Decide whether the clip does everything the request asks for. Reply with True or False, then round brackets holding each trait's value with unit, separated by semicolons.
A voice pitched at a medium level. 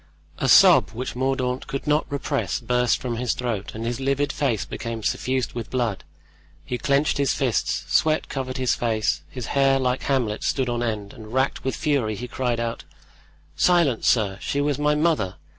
False (125 Hz)